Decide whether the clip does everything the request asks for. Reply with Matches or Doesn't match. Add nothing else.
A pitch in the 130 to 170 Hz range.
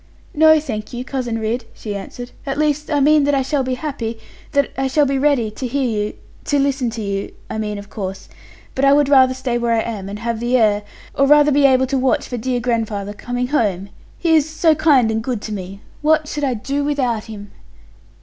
Doesn't match